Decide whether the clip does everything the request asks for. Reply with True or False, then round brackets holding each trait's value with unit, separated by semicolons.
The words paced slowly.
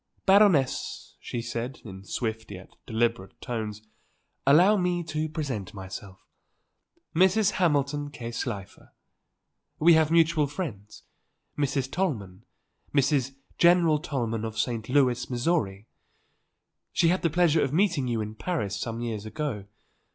True (125 wpm)